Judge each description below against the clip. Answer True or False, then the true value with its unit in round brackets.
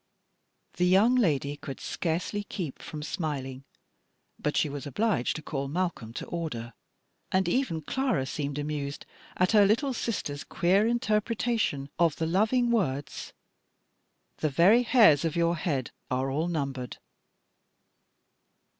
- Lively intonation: True (6.6 semitones)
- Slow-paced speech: True (130 wpm)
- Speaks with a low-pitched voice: False (165 Hz)